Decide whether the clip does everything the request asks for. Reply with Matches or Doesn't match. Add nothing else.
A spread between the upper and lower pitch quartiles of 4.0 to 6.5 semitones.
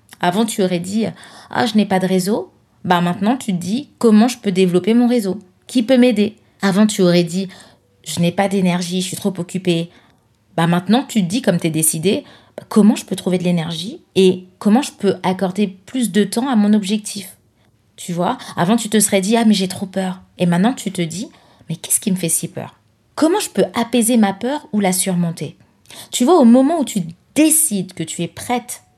Matches